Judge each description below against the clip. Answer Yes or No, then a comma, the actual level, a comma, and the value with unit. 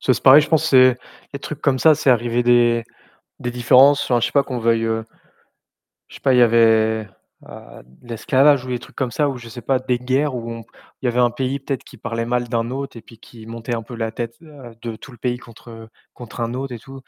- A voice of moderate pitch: No, low, 120 Hz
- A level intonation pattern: Yes, narrow, 2.3 semitones